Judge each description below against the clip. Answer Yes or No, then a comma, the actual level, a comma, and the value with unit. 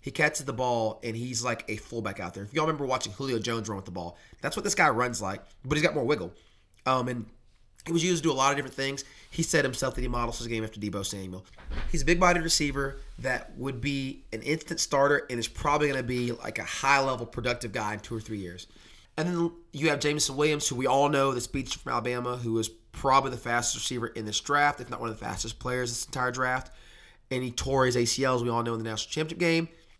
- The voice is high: No, low, 125 Hz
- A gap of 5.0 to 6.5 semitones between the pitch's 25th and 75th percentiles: No, average, 3.8 semitones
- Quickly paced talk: Yes, fast, 260 wpm